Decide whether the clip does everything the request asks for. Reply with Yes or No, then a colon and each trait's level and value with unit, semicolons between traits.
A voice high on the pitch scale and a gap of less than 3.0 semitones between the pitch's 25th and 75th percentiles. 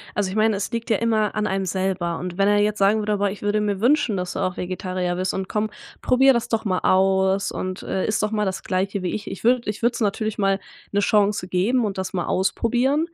Yes: high, 205 Hz; narrow, 2.4 semitones